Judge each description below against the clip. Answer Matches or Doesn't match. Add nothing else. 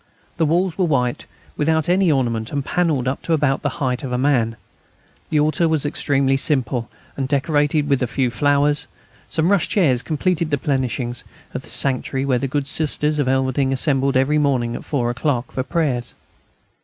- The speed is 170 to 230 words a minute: Matches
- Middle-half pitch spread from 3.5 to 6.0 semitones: Doesn't match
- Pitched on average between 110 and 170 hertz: Matches